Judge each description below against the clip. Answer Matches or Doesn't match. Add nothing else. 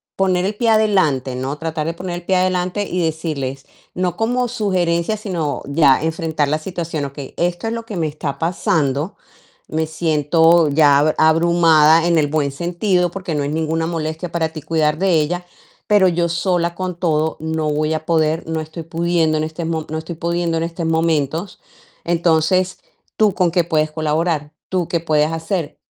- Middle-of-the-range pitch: Matches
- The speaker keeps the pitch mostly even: Matches